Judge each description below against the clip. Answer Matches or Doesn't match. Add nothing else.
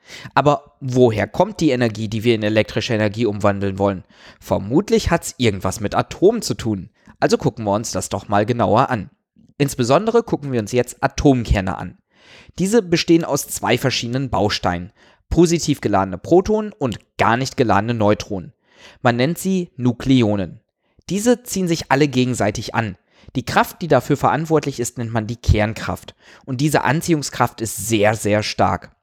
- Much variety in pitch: Matches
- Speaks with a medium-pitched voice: Doesn't match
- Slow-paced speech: Doesn't match